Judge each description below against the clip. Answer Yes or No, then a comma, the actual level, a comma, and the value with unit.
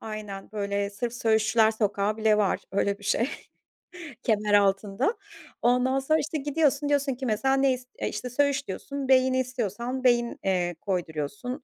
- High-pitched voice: Yes, high, 235 Hz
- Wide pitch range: No, average, 4.4 semitones